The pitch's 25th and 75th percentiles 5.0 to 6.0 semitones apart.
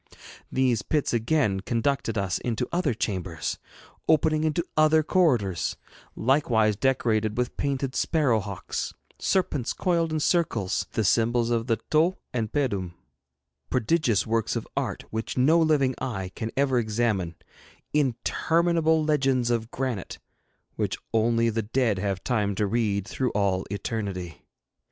Yes: wide, 5.6 semitones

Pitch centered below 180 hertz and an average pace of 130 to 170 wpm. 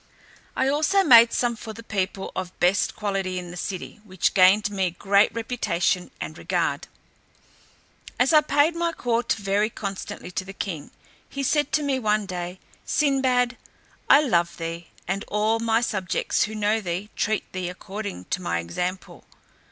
No: high, 205 Hz; average, 160 wpm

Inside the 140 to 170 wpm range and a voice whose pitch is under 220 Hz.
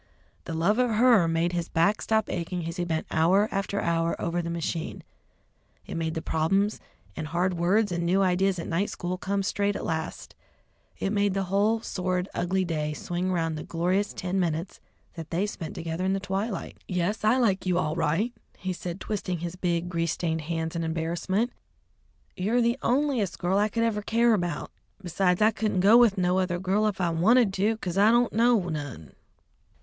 No: average, 195 wpm; medium, 185 Hz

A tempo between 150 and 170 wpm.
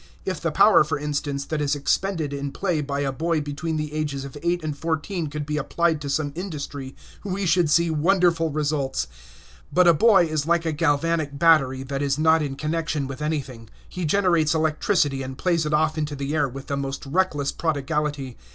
No: average, 195 wpm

